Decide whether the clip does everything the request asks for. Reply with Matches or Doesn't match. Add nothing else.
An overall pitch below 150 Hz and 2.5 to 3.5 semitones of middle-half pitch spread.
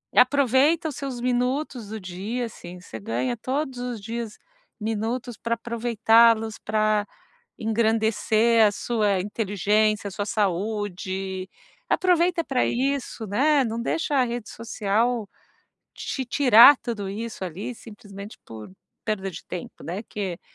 Doesn't match